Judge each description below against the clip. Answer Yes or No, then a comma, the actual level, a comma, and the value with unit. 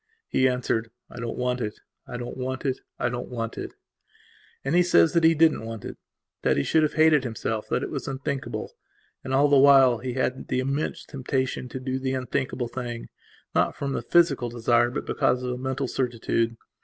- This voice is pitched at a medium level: No, low, 130 Hz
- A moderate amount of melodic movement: No, narrow, 2.2 semitones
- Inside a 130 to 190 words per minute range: No, fast, 205 wpm